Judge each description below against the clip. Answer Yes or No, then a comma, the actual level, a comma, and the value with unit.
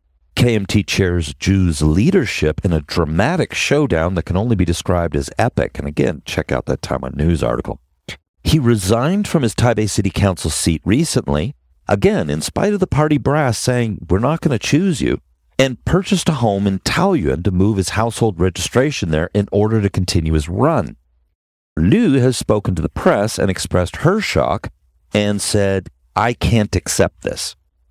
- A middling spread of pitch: No, wide, 6.5 semitones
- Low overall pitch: Yes, very low, 95 Hz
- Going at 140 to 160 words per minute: No, average, 170 wpm